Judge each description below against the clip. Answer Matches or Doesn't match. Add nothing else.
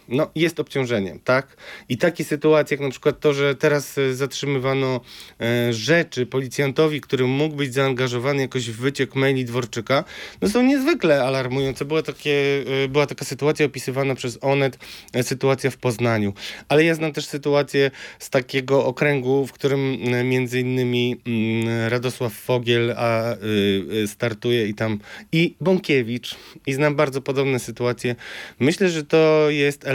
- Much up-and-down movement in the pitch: Doesn't match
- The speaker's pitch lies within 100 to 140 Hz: Matches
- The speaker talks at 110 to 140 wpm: Matches